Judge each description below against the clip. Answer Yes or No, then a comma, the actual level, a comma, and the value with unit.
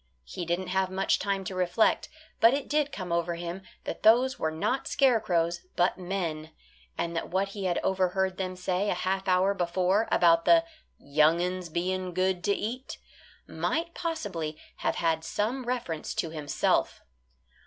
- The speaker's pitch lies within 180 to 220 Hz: Yes, medium, 185 Hz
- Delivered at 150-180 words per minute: Yes, average, 165 wpm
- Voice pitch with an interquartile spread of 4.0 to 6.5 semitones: No, average, 3.0 semitones